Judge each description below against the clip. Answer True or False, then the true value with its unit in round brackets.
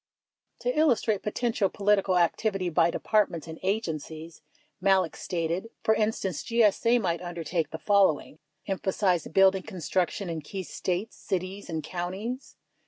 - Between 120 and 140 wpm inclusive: True (135 wpm)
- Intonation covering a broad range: False (3.6 semitones)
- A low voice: False (190 Hz)